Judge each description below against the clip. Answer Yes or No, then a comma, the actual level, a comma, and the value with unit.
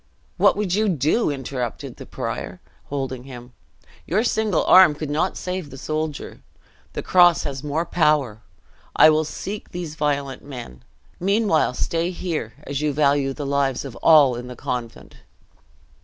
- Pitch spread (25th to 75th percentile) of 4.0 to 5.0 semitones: Yes, average, 4.3 semitones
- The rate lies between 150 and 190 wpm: Yes, average, 155 wpm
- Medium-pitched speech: Yes, medium, 150 Hz